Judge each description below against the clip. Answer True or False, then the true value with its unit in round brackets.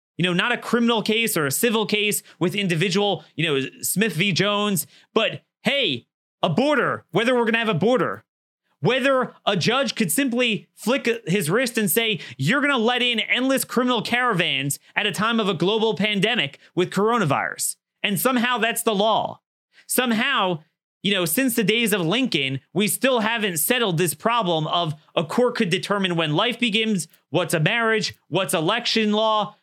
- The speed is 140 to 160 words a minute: False (175 wpm)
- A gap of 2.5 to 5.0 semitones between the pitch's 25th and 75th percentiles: True (4.6 semitones)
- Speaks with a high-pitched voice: True (210 Hz)